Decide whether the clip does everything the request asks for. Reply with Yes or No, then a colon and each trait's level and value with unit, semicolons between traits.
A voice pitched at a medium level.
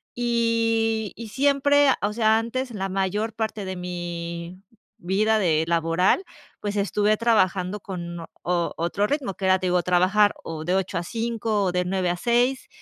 No: high, 200 Hz